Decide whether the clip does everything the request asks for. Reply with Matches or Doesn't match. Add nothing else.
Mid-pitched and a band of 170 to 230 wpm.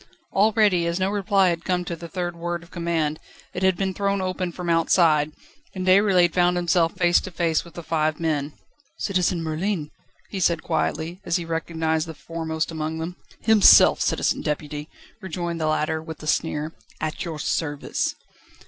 Matches